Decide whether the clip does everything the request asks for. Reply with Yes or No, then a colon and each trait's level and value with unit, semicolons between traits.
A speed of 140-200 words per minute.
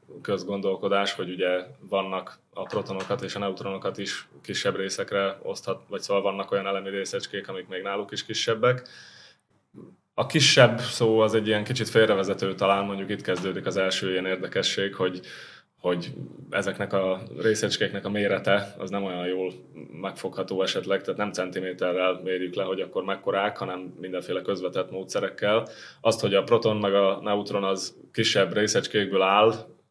Yes: average, 150 wpm